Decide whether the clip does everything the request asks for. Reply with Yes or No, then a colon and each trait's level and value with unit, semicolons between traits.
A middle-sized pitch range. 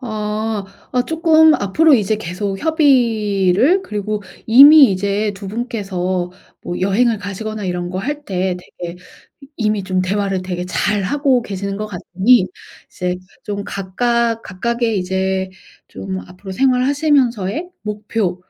Yes: average, 4.3 semitones